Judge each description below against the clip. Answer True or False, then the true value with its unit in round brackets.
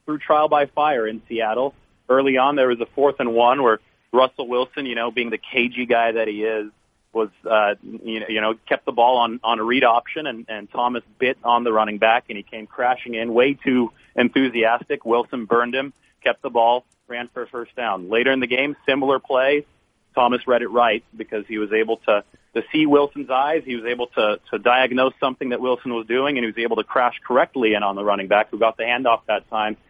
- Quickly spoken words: True (230 wpm)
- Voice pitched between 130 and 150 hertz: False (120 Hz)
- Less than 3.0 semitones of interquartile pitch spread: True (2.6 semitones)